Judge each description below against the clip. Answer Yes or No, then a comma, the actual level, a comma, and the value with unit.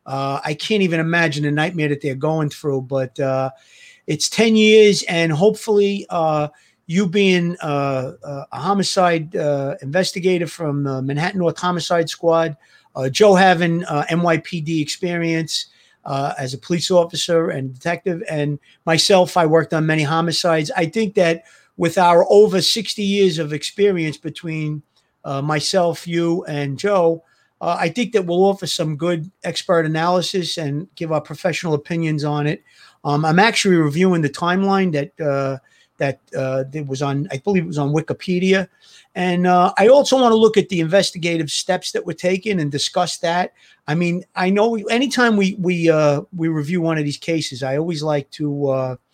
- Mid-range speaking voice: Yes, medium, 165 Hz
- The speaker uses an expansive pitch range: No, average, 3.6 semitones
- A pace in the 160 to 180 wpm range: Yes, average, 170 wpm